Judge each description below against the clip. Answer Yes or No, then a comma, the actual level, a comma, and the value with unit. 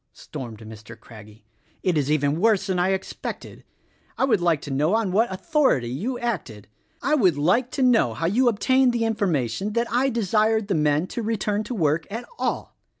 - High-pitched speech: Yes, high, 195 Hz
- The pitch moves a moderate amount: No, wide, 7.8 semitones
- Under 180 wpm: No, average, 190 wpm